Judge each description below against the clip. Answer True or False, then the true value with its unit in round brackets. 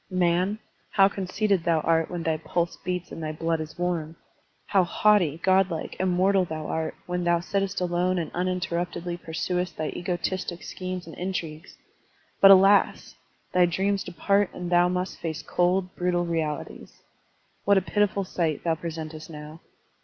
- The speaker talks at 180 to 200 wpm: False (155 wpm)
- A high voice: False (175 Hz)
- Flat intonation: True (2.3 semitones)